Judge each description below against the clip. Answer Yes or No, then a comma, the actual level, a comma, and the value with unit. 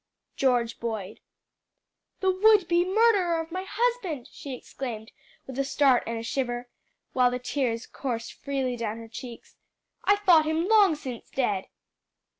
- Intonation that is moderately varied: No, wide, 6.8 semitones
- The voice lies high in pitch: Yes, very high, 270 Hz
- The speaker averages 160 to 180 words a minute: No, average, 145 wpm